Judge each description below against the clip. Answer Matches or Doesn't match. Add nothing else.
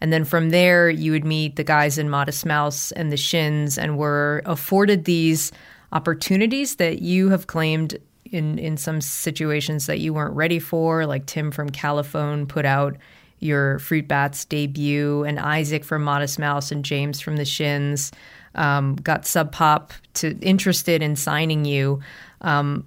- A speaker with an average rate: Matches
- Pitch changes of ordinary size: Doesn't match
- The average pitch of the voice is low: Doesn't match